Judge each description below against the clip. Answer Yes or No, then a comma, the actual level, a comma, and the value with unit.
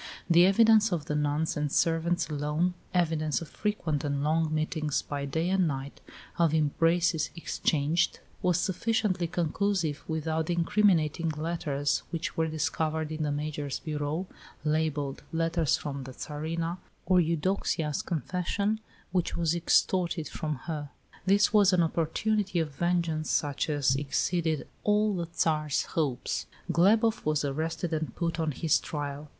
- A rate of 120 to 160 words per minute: Yes, average, 140 wpm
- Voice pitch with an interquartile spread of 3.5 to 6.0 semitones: No, narrow, 2.6 semitones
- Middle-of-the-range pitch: Yes, medium, 160 Hz